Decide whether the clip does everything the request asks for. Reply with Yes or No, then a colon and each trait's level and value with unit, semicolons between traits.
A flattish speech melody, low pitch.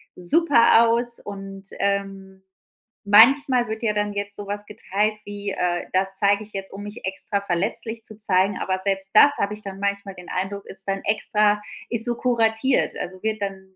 No: narrow, 2.0 semitones; high, 200 Hz